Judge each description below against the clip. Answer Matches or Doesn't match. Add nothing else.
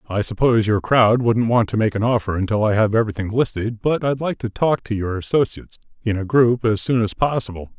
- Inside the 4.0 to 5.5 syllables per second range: Doesn't match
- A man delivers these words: Matches